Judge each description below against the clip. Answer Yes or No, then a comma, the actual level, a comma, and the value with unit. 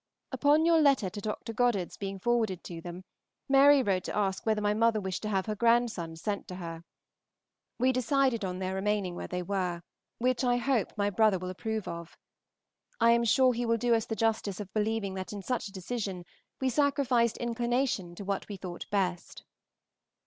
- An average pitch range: Yes, average, 4.2 semitones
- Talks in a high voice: Yes, high, 210 Hz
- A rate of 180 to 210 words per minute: Yes, average, 190 wpm